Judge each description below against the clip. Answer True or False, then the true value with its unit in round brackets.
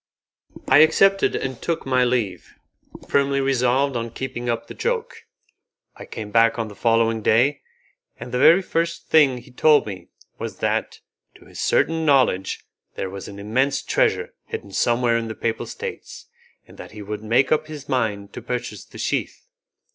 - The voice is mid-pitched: False (125 Hz)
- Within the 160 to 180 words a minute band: True (170 wpm)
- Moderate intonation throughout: True (4.2 semitones)